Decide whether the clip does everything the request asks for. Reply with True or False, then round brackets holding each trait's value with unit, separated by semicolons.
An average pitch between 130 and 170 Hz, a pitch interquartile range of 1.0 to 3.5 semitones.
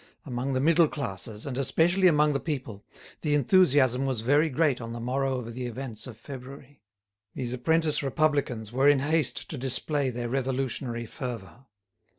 True (135 Hz; 3.1 semitones)